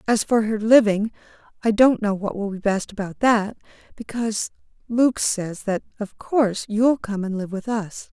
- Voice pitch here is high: Yes, high, 215 Hz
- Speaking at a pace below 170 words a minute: No, average, 185 wpm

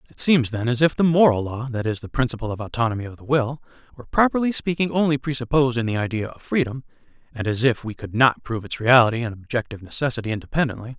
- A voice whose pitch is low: Yes, low, 125 Hz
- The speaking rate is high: Yes, fast, 220 wpm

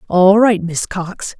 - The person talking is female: Yes, female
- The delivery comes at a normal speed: Yes, average, 170 wpm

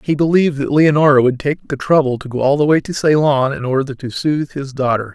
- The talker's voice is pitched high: No, medium, 140 Hz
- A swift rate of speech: Yes, fast, 245 wpm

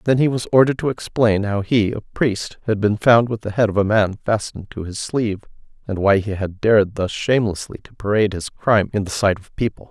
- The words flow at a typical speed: No, fast, 235 wpm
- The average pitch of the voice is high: No, low, 105 Hz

